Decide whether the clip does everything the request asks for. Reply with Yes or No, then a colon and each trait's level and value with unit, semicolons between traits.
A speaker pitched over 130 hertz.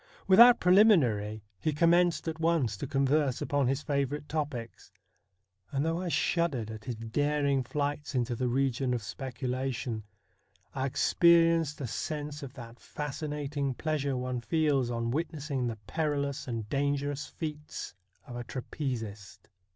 Yes: medium, 140 Hz